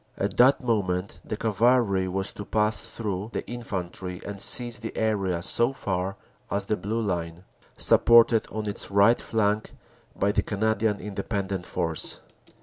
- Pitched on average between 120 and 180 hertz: No, low, 105 Hz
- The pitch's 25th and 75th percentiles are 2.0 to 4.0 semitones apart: Yes, average, 2.8 semitones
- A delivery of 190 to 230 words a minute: No, average, 145 wpm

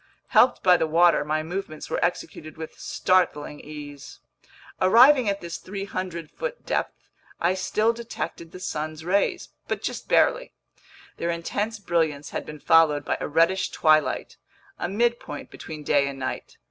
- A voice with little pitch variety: No, average, 4.2 semitones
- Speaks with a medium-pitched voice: Yes, medium, 170 Hz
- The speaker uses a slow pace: No, average, 150 wpm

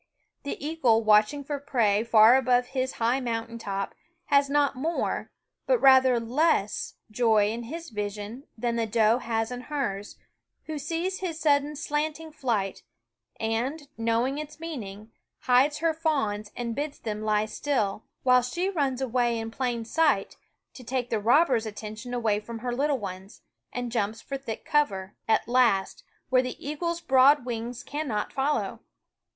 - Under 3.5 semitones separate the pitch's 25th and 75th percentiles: No, average, 4.5 semitones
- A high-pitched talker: Yes, high, 245 Hz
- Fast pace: No, average, 155 wpm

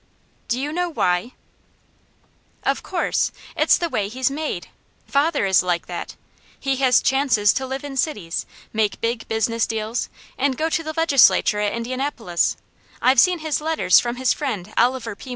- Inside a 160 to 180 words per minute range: Yes, average, 165 wpm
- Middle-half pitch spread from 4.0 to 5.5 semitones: Yes, average, 4.9 semitones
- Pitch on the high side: Yes, very high, 255 Hz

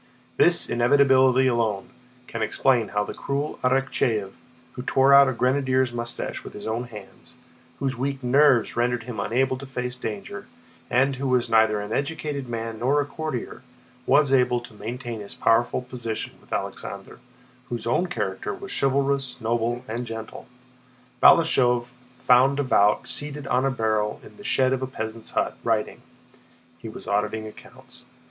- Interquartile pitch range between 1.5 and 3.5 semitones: Yes, average, 3.0 semitones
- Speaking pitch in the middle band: No, low, 125 Hz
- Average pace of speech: Yes, average, 155 wpm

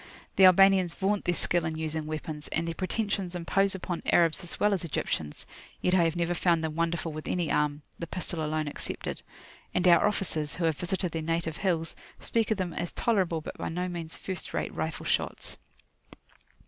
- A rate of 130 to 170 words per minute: No, average, 195 wpm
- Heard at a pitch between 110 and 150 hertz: No, medium, 170 Hz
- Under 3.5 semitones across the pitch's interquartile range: Yes, narrow, 2.6 semitones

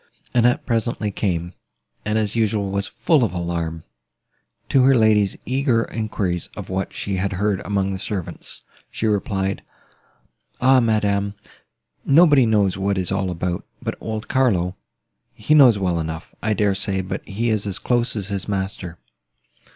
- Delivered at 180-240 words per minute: No, average, 160 wpm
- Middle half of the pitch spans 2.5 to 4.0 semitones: Yes, average, 3.0 semitones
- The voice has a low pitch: Yes, low, 100 Hz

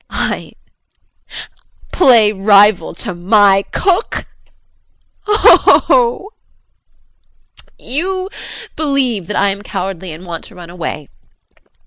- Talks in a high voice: Yes, high, 205 Hz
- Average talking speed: No, slow, 100 wpm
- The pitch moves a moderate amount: No, wide, 7.3 semitones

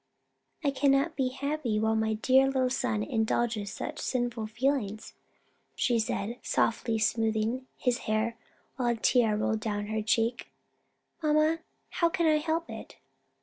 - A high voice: Yes, high, 240 Hz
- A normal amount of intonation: Yes, average, 3.9 semitones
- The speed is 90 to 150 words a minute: Yes, average, 145 wpm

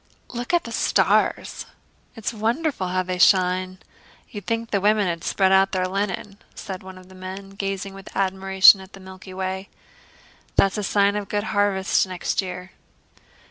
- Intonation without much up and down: Yes, narrow, 1.6 semitones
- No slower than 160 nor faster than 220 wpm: Yes, average, 180 wpm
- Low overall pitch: No, high, 195 Hz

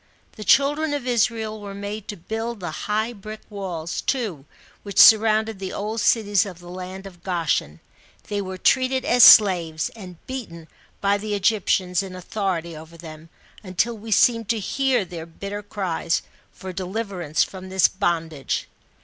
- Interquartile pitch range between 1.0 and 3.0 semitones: No, average, 3.8 semitones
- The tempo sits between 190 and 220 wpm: No, average, 160 wpm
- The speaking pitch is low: No, high, 200 Hz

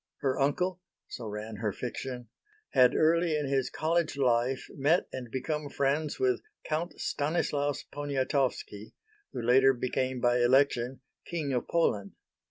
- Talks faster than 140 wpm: No, slow, 135 wpm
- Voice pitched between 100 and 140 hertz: Yes, low, 135 Hz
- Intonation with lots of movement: No, average, 3.6 semitones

